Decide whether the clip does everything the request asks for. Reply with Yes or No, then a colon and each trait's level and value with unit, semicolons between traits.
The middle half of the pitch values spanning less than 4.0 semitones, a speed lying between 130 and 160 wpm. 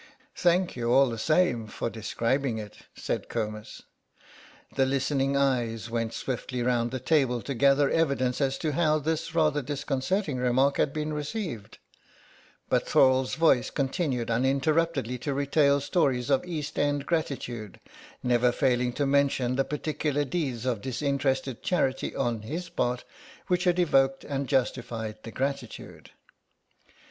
Yes: average, 3.3 semitones; average, 140 wpm